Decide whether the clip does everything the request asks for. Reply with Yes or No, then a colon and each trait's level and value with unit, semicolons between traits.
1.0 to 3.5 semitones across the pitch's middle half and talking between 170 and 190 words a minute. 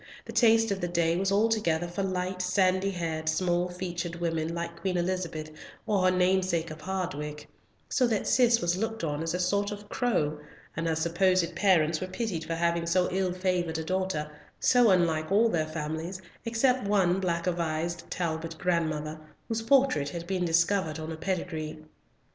Yes: average, 2.8 semitones; average, 175 wpm